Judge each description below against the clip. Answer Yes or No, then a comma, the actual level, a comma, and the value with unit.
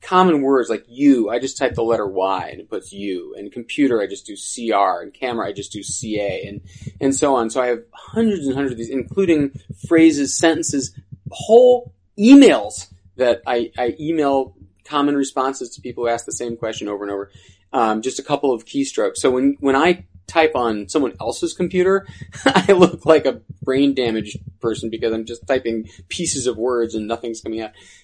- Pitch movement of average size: No, wide, 6.3 semitones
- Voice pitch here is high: No, low, 135 Hz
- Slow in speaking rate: No, average, 200 wpm